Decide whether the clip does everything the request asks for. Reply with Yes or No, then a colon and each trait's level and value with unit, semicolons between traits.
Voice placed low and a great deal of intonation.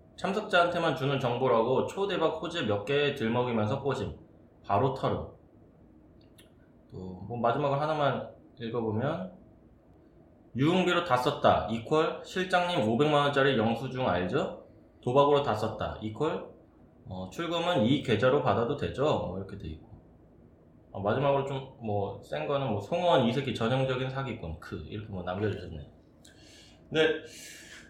Yes: low, 120 Hz; wide, 6.2 semitones